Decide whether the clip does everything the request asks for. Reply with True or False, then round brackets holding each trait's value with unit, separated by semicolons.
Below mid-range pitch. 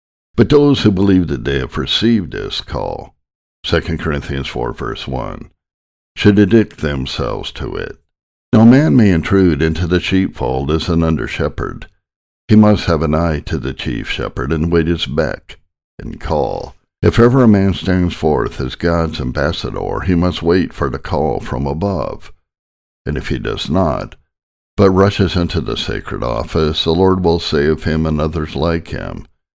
True (85 Hz)